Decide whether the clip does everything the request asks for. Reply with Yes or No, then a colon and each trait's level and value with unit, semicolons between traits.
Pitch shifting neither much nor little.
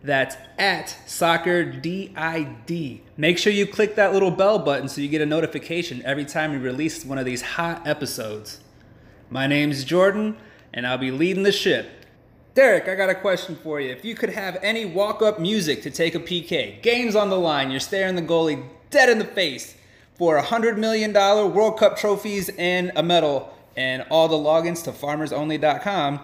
No: wide, 5.7 semitones